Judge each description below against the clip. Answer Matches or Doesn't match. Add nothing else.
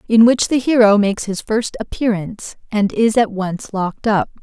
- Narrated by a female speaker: Matches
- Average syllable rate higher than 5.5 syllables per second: Doesn't match